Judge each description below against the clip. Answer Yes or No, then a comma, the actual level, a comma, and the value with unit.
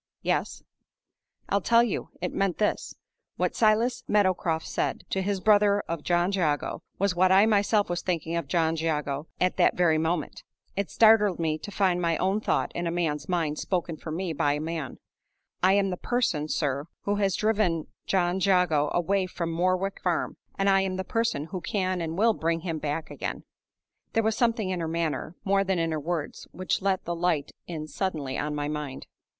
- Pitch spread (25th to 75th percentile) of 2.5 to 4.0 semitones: Yes, average, 3.5 semitones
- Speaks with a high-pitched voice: No, medium, 180 Hz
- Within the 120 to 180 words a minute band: No, average, 195 wpm